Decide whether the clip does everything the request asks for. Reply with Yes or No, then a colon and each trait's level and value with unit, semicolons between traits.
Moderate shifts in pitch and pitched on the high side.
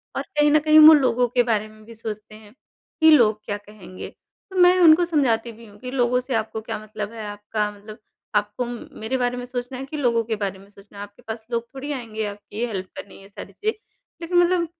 Yes: average, 3.9 semitones; high, 230 Hz